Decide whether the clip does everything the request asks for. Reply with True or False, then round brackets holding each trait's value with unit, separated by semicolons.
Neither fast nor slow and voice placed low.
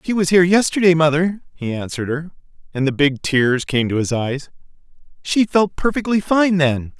False (180 wpm; 160 Hz)